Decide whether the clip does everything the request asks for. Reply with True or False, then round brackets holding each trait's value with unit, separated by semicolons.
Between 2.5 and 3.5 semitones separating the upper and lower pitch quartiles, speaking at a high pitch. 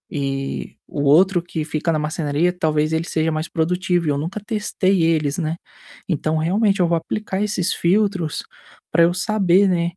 False (3.2 semitones; 170 Hz)